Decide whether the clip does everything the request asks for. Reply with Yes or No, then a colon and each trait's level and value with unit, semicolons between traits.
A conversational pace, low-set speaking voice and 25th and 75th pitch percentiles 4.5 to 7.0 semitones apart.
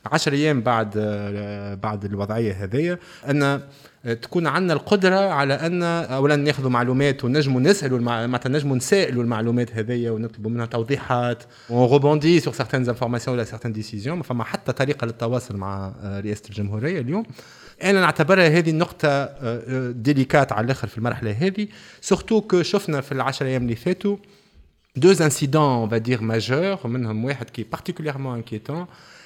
No: slow, 140 wpm; low, 130 Hz; average, 5.2 semitones